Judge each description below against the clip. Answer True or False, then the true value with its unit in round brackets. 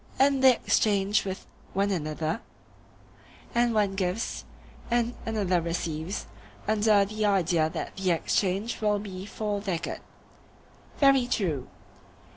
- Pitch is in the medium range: False (200 Hz)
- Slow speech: True (120 wpm)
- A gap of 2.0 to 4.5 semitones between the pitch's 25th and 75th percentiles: True (3.2 semitones)